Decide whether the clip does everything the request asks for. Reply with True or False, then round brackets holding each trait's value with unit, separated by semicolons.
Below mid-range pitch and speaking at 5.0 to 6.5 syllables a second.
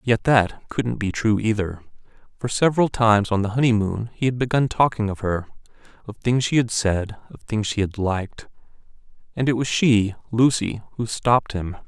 True (110 Hz; 5.1 syllables/s)